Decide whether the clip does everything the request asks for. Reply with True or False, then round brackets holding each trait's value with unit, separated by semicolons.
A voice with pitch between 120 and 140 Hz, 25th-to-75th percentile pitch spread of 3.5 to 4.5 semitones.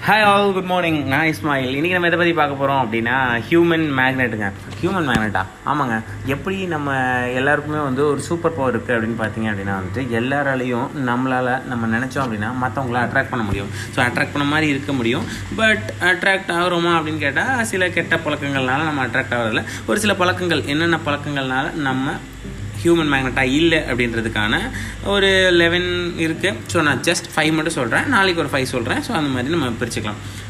False (135 Hz; 5.4 semitones)